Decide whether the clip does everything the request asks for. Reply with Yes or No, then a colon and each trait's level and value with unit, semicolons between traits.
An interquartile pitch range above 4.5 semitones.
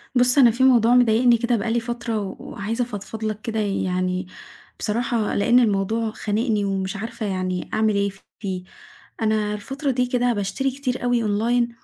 No: average, 3.0 semitones